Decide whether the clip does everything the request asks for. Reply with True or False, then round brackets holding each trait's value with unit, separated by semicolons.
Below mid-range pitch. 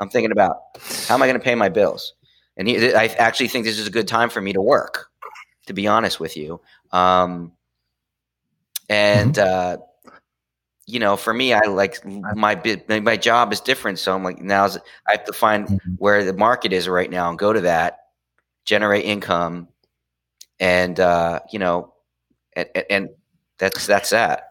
True (95 Hz)